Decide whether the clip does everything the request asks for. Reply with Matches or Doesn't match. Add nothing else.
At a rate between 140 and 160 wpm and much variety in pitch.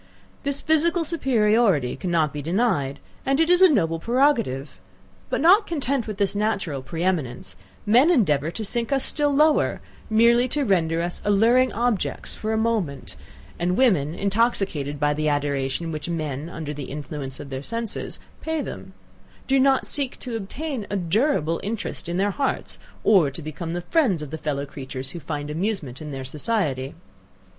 Doesn't match